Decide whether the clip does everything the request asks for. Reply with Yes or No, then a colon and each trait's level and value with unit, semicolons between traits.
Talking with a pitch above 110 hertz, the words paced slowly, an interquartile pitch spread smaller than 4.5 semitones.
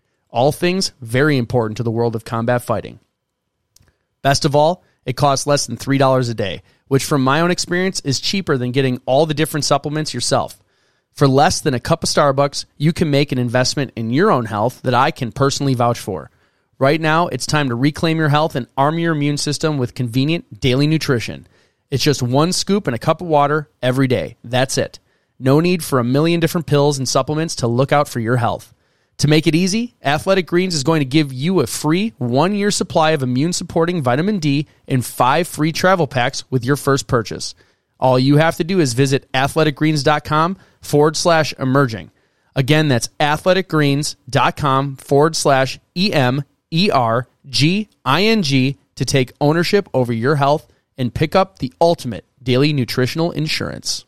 No: medium, 140 Hz; average, 190 wpm; average, 3.8 semitones